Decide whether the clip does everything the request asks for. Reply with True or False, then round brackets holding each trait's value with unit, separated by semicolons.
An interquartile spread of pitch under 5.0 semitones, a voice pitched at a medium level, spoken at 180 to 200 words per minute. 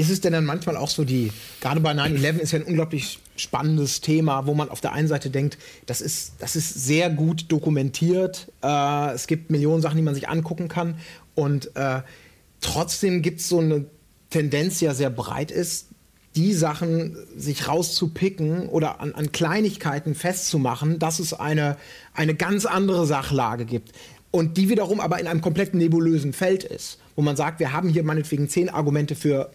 True (2.8 semitones; 155 Hz; 185 wpm)